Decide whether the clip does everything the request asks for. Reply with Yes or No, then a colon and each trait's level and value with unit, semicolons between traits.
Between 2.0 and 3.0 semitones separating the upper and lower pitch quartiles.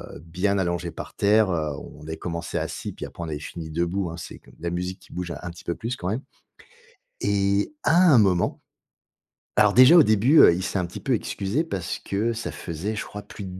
No: average, 3.8 semitones